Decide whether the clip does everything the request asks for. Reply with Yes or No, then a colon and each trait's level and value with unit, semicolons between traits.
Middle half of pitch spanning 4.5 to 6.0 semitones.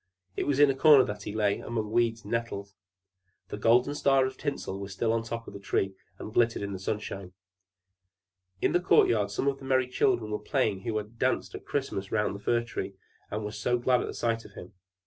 No: average, 3.7 semitones